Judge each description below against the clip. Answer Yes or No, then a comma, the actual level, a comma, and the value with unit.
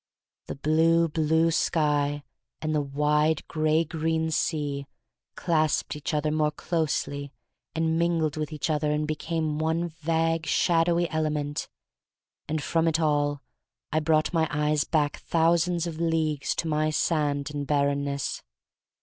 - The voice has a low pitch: No, medium, 155 Hz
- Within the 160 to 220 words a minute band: No, average, 140 wpm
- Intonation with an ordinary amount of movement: No, narrow, 1.6 semitones